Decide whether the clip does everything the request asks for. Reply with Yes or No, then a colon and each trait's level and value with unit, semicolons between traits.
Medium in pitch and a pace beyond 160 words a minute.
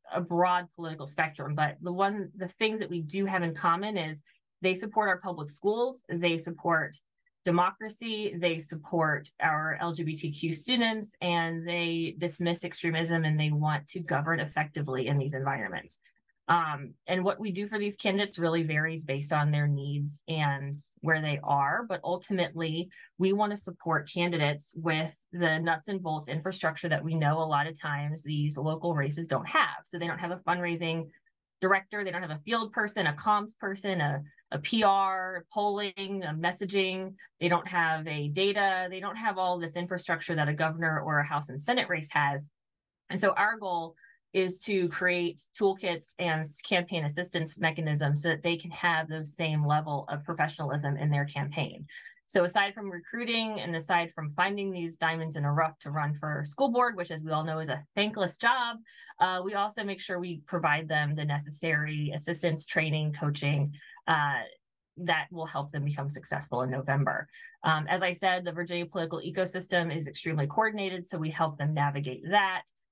Yes: medium, 165 Hz; average, 180 wpm